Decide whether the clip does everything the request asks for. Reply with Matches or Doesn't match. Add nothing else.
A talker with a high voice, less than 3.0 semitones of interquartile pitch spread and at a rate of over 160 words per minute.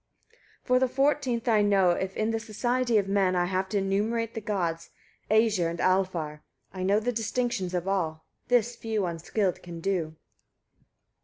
Doesn't match